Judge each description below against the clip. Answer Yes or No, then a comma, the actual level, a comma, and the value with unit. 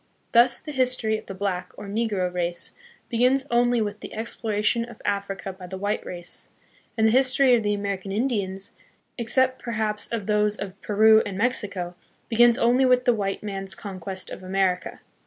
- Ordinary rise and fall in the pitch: Yes, average, 3.5 semitones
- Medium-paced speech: Yes, average, 175 wpm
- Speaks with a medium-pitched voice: No, high, 210 Hz